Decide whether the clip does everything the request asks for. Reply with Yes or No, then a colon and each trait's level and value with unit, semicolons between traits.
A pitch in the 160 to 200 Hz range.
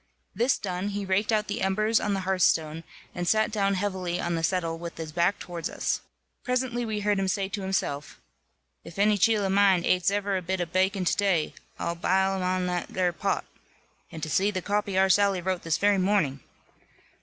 Yes: high, 190 Hz